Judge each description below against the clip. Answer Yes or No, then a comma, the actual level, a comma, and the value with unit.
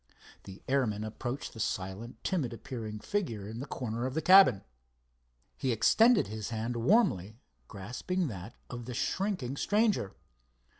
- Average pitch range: No, wide, 6.7 semitones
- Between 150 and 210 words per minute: No, average, 140 wpm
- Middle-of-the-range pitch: No, low, 120 Hz